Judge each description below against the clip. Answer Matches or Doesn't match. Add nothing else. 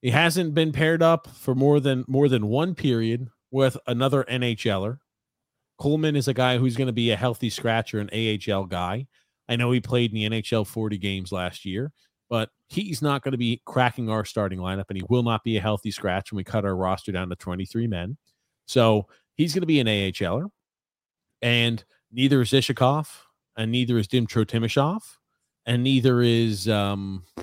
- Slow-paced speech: Doesn't match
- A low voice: Matches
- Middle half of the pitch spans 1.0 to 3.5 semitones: Doesn't match